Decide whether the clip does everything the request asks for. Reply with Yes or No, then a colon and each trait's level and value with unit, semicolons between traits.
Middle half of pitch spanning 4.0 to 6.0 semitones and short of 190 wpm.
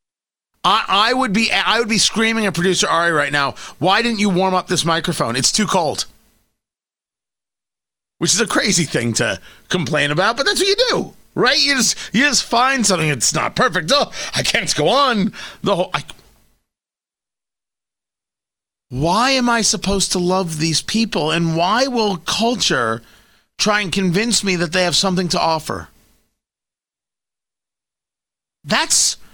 Yes: average, 5.0 semitones; average, 155 wpm